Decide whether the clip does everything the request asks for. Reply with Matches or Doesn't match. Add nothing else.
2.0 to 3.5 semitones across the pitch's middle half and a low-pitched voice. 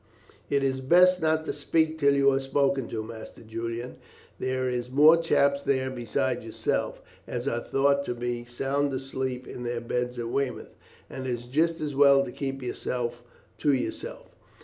Matches